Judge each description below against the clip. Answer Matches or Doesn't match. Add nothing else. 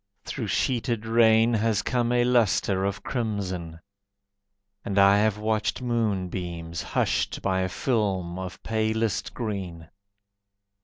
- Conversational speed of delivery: Doesn't match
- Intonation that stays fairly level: Doesn't match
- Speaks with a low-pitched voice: Matches